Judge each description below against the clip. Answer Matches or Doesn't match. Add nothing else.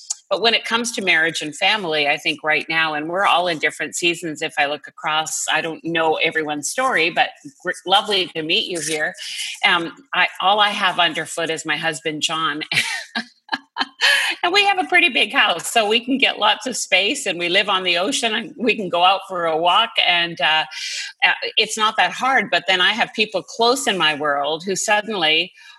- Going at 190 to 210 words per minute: Matches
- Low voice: Doesn't match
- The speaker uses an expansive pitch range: Matches